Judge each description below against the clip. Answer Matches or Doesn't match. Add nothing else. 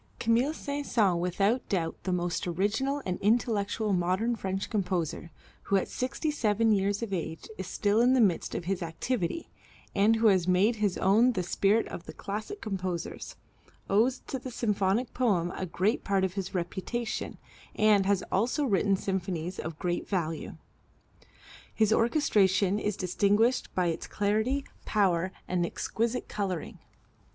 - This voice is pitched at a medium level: Doesn't match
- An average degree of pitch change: Matches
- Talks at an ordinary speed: Matches